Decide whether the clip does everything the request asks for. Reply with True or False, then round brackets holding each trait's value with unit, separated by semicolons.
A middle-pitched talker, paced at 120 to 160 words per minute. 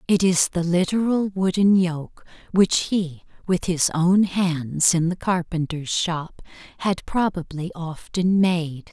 True (175 Hz; 135 wpm)